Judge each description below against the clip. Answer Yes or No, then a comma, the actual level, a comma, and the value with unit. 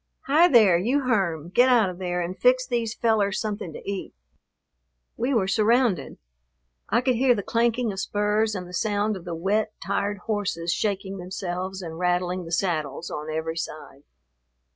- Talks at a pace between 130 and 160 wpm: No, average, 170 wpm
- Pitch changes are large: No, average, 4.0 semitones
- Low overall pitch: No, high, 200 Hz